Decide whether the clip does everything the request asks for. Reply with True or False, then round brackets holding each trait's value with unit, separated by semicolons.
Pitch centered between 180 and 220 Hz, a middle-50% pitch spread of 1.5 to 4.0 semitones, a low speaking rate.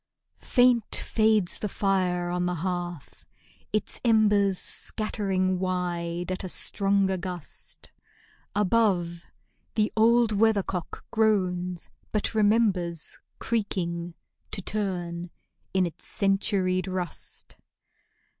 True (190 Hz; 3.2 semitones; 95 wpm)